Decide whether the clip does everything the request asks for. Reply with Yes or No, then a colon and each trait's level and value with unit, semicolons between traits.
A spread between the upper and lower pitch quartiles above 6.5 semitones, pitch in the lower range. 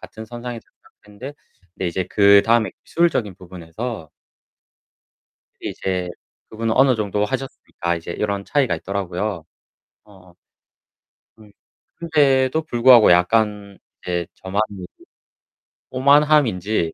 No: average, 5.2 semitones; low, 105 Hz